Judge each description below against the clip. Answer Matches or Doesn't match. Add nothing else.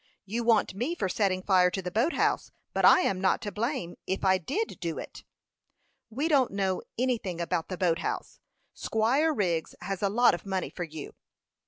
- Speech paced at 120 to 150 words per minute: Doesn't match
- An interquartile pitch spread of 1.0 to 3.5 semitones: Doesn't match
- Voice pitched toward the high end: Matches